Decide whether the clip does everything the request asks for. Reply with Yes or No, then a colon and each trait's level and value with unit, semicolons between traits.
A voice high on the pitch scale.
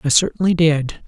No: medium, 165 Hz